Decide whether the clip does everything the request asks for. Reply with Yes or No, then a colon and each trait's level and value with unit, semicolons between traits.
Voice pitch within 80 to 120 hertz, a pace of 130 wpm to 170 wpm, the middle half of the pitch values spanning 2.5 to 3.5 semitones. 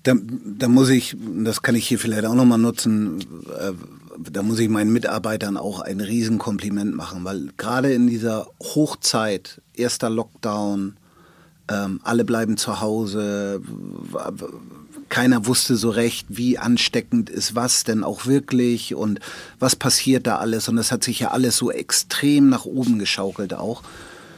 Yes: low, 115 Hz; average, 155 wpm; average, 2.9 semitones